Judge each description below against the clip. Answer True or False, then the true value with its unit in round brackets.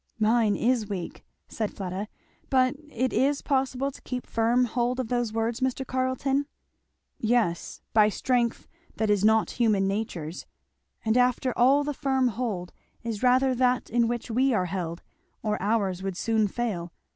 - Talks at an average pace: True (155 wpm)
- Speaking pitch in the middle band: False (235 Hz)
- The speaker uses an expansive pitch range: False (3.4 semitones)